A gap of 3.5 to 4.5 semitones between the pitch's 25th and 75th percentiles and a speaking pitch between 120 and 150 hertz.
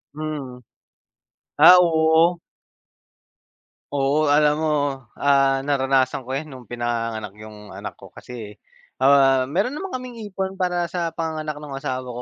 Yes: average, 4.1 semitones; medium, 140 Hz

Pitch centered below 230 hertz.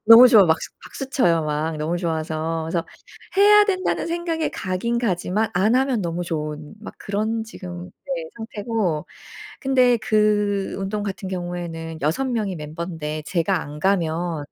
Yes: medium, 185 Hz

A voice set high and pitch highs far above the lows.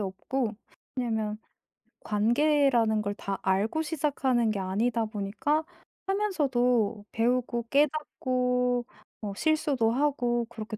No: high, 240 Hz; average, 4.3 semitones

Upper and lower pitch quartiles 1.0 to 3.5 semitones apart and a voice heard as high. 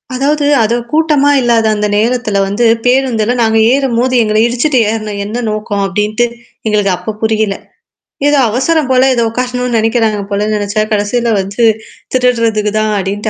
Yes: average, 2.9 semitones; high, 225 Hz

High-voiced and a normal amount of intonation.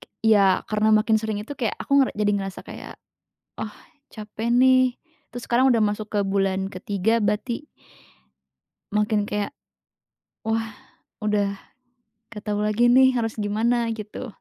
No: high, 215 Hz; narrow, 2.1 semitones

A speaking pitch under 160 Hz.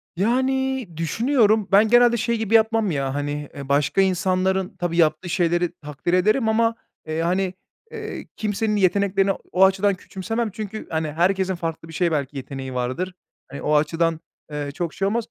No: medium, 185 Hz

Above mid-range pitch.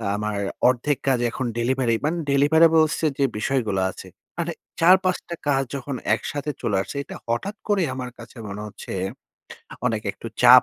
No: low, 135 Hz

